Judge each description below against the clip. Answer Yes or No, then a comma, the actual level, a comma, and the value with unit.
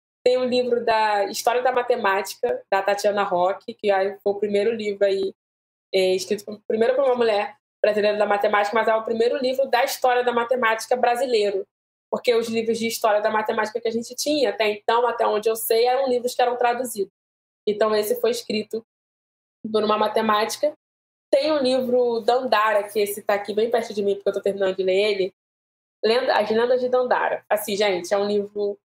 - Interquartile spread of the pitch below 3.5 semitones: Yes, average, 2.9 semitones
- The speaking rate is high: Yes, fast, 200 wpm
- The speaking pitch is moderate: No, high, 220 Hz